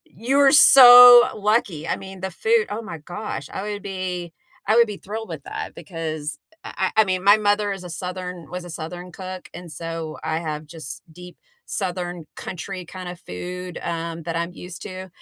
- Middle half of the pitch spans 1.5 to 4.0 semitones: Yes, average, 3.4 semitones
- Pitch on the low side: No, medium, 180 Hz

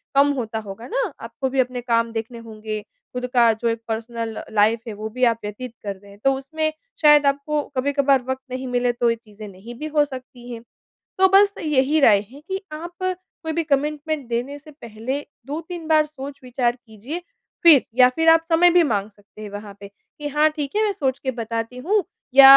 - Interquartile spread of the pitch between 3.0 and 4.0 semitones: No, average, 4.8 semitones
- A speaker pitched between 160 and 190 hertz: No, very high, 260 Hz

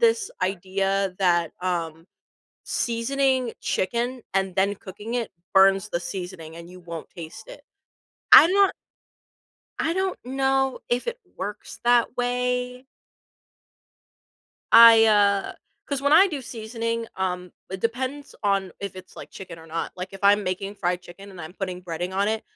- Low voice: No, high, 200 Hz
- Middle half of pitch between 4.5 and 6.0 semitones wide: Yes, average, 5.2 semitones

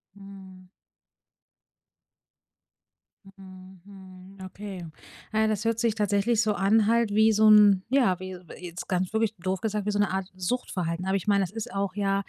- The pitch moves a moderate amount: No, narrow, 2.3 semitones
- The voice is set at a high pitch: Yes, high, 195 Hz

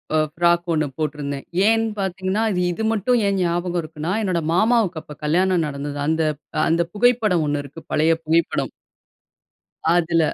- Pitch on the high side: No, medium, 170 Hz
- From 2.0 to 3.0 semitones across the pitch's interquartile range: No, average, 3.5 semitones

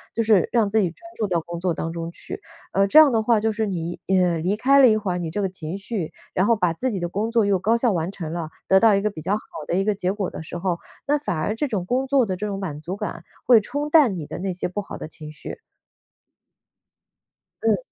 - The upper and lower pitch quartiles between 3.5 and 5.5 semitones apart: Yes, average, 4.3 semitones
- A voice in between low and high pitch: No, high, 195 Hz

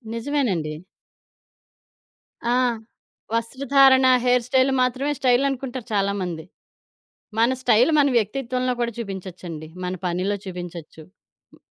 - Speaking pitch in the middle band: No, high, 235 Hz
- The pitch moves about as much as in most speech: No, wide, 5.9 semitones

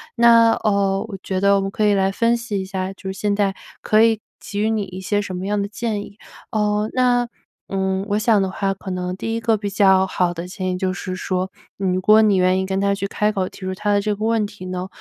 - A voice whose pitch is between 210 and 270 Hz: No, high, 200 Hz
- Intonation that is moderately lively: No, narrow, 2.0 semitones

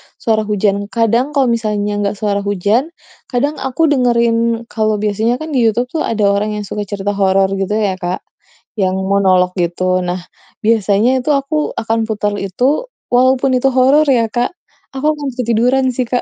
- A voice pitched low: No, high, 225 Hz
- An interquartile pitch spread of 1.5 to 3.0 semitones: No, average, 3.9 semitones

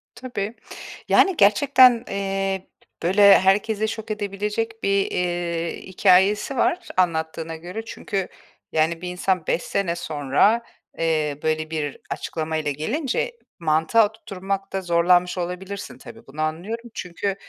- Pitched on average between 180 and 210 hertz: Yes, high, 190 Hz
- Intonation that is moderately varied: Yes, average, 4.1 semitones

